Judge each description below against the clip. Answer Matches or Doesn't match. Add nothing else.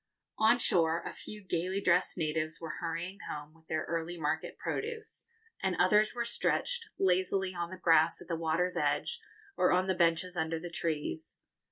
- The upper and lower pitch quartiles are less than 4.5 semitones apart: Matches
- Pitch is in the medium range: Matches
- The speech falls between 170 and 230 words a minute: Matches